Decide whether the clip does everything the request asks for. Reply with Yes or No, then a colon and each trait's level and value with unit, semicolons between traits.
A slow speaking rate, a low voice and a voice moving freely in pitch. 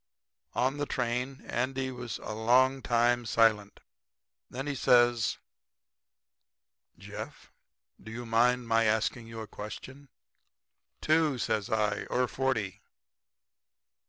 No: slow, 110 wpm; low, 120 Hz; average, 2.7 semitones